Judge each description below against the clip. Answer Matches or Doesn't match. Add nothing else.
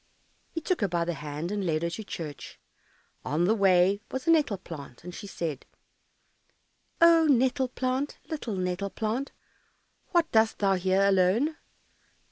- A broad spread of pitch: Matches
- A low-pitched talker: Doesn't match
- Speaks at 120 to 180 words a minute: Matches